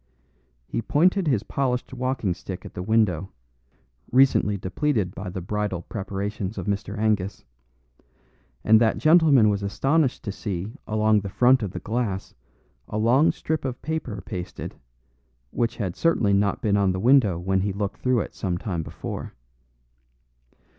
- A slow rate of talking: No, average, 155 wpm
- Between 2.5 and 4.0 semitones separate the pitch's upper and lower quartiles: No, average, 4.4 semitones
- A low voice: Yes, low, 105 Hz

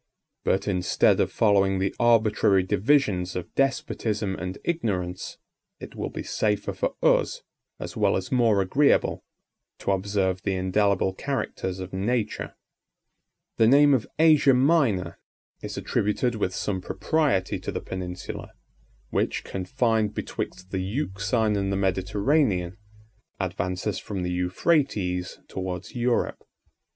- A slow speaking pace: Yes, slow, 125 wpm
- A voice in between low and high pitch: No, low, 100 Hz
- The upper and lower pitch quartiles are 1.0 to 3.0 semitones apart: No, average, 4.2 semitones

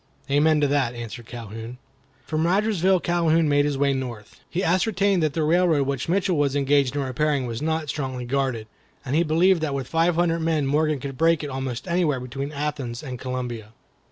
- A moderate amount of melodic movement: Yes, average, 4.0 semitones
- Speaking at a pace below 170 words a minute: No, average, 190 wpm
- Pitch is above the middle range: No, medium, 145 Hz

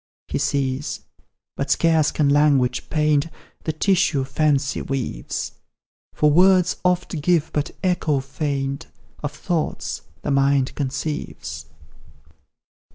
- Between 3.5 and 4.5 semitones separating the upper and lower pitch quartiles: No, average, 2.8 semitones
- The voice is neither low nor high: Yes, medium, 150 Hz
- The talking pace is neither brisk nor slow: No, slow, 105 wpm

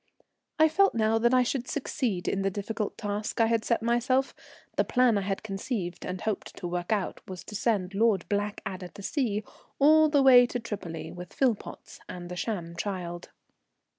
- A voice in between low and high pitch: No, high, 210 Hz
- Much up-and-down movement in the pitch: No, average, 4.6 semitones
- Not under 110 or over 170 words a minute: No, average, 185 wpm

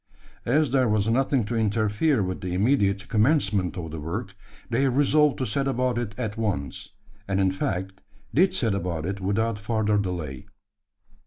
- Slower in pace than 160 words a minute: No, average, 165 wpm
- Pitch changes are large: No, average, 4.7 semitones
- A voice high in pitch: No, low, 105 Hz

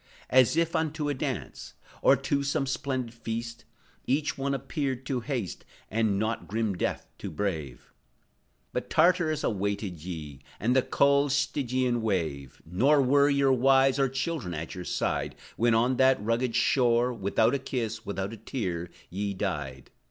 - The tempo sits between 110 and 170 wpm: Yes, average, 160 wpm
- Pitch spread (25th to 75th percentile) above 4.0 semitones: Yes, average, 5.3 semitones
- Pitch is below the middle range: Yes, low, 120 Hz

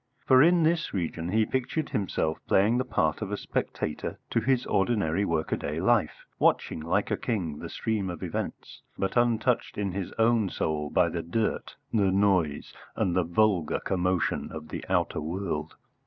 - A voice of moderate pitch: No, very low, 95 Hz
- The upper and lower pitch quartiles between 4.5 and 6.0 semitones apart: Yes, wide, 5.4 semitones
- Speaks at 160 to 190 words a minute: Yes, average, 170 wpm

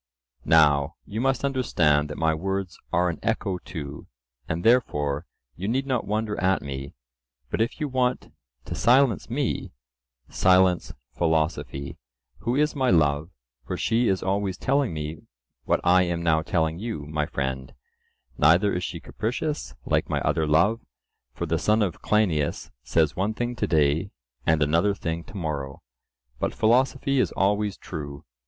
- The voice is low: Yes, very low, 90 Hz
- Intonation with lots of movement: Yes, wide, 6.4 semitones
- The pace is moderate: Yes, average, 155 wpm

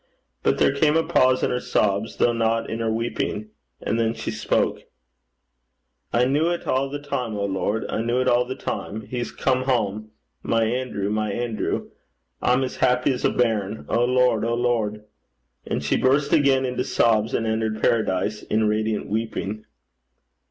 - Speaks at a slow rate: No, average, 175 wpm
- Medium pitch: No, low, 115 Hz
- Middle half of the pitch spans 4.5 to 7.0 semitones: No, average, 2.8 semitones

